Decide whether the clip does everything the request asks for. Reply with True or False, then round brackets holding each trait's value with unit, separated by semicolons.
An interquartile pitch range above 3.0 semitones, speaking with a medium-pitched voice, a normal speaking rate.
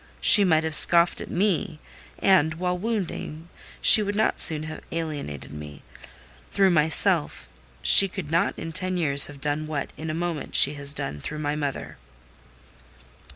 True (3.5 semitones; 160 Hz; 160 wpm)